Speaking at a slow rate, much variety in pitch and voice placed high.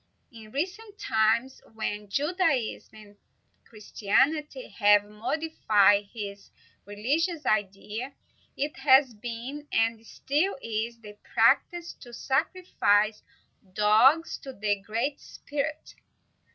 Yes: slow, 100 wpm; wide, 5.9 semitones; high, 235 Hz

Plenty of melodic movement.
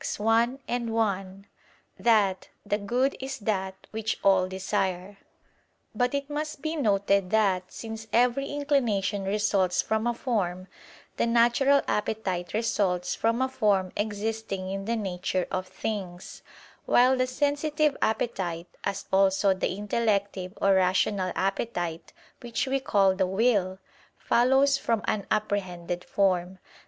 No: average, 3.9 semitones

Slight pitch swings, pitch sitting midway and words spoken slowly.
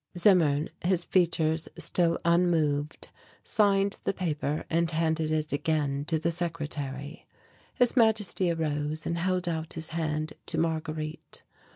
Yes: narrow, 2.2 semitones; medium, 160 Hz; slow, 130 wpm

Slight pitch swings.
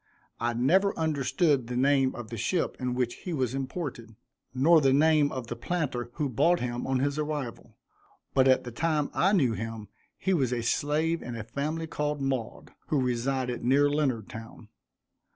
No: average, 3.9 semitones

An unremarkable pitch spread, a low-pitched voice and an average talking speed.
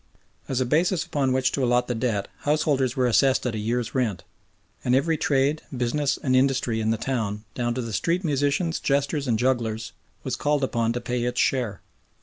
Yes: average, 3.0 semitones; low, 130 Hz; average, 195 wpm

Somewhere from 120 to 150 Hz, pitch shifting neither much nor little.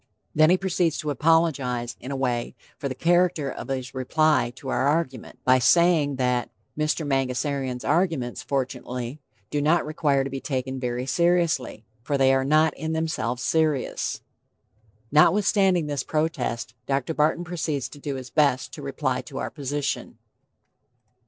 Yes: medium, 140 Hz; average, 3.6 semitones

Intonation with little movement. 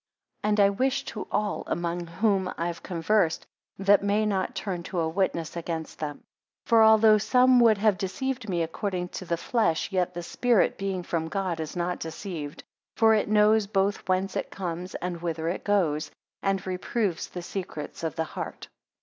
No: average, 3.7 semitones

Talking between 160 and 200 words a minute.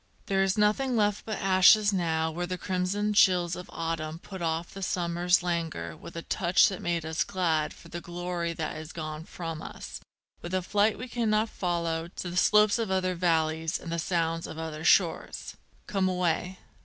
Yes: average, 190 wpm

